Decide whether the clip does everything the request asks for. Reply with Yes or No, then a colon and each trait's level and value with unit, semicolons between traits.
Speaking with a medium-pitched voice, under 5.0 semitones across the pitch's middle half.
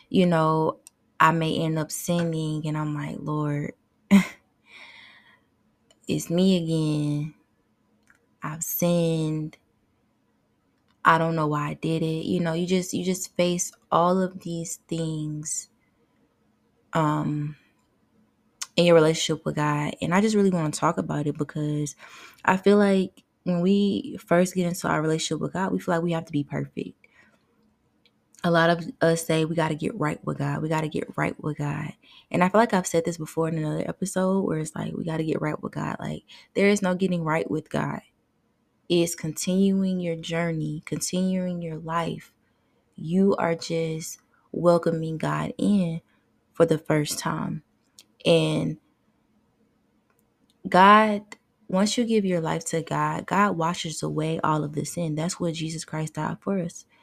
Yes: medium, 165 Hz; average, 2.7 semitones